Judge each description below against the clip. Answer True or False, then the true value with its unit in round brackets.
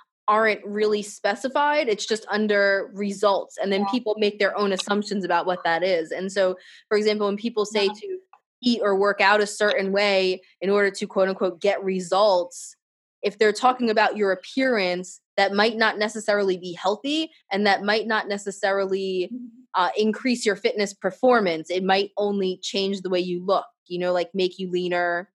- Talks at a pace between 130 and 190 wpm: True (180 wpm)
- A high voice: True (200 Hz)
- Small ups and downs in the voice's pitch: True (2.0 semitones)